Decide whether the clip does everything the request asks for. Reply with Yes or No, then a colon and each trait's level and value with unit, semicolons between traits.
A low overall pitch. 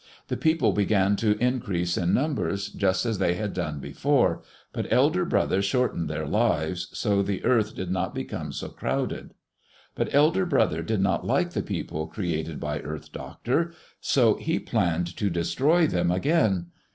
Yes: low, 100 Hz